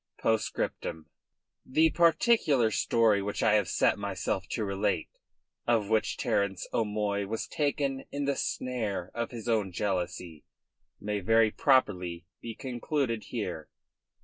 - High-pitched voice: No, low, 110 Hz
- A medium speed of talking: No, slow, 130 wpm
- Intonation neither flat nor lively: Yes, average, 3.9 semitones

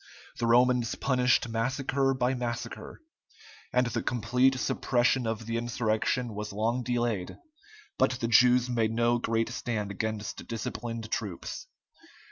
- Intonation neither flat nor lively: No, narrow, 1.7 semitones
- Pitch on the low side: Yes, low, 120 Hz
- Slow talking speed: Yes, slow, 125 wpm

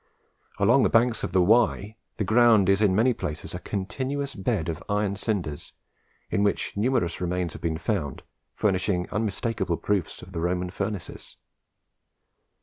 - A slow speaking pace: No, average, 150 wpm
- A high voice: No, low, 100 Hz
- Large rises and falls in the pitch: No, average, 3.7 semitones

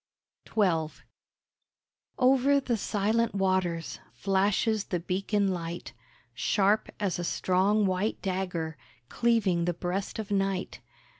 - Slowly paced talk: Yes, slow, 105 wpm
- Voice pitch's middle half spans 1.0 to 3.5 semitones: Yes, average, 2.9 semitones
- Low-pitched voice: No, high, 195 Hz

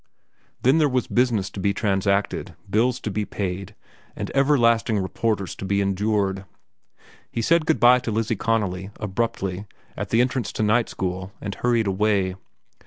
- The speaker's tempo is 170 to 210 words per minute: No, average, 160 wpm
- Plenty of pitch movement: No, average, 3.3 semitones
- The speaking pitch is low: Yes, low, 105 Hz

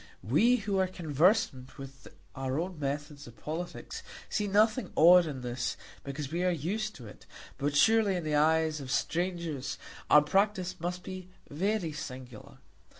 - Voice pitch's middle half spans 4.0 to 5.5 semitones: Yes, average, 5.0 semitones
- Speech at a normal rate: Yes, average, 155 wpm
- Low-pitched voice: No, medium, 160 Hz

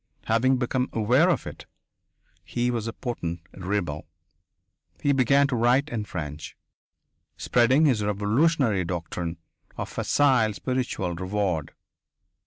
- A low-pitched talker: Yes, low, 110 Hz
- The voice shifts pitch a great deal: Yes, wide, 5.9 semitones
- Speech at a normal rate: No, slow, 115 wpm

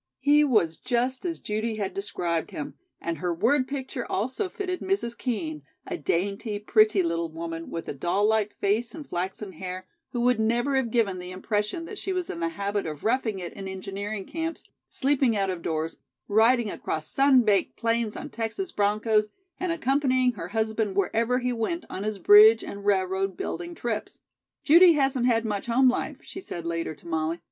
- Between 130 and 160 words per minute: No, average, 185 wpm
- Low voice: No, high, 215 Hz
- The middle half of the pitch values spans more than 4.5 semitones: Yes, average, 5.2 semitones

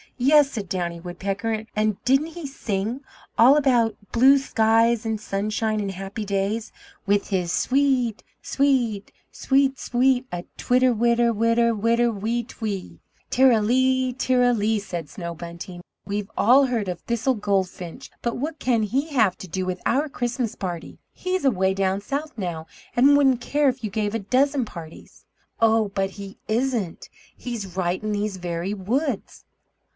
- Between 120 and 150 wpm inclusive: No, average, 165 wpm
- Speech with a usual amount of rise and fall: Yes, average, 4.6 semitones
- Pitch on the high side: Yes, high, 225 Hz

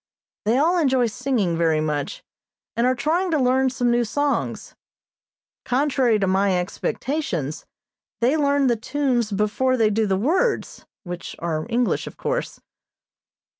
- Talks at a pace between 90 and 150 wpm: Yes, average, 140 wpm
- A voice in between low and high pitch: No, high, 245 Hz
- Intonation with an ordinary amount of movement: No, wide, 5.8 semitones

